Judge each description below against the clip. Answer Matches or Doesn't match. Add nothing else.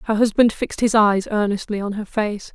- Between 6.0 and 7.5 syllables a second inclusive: Doesn't match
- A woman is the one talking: Matches